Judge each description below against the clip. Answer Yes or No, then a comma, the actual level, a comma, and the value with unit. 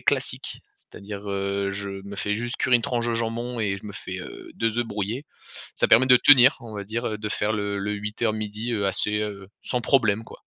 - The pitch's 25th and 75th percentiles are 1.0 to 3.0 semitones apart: Yes, narrow, 2.6 semitones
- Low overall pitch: Yes, low, 105 Hz